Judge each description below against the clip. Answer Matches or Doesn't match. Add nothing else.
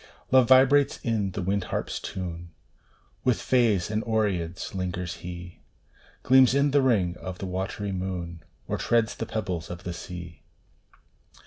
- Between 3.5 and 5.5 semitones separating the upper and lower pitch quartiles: Matches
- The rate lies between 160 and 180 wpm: Doesn't match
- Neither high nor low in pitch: Doesn't match